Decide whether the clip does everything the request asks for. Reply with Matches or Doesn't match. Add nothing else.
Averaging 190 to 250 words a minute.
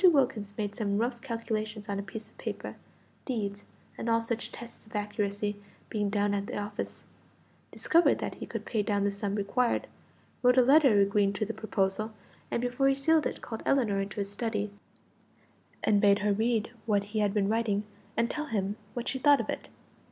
Matches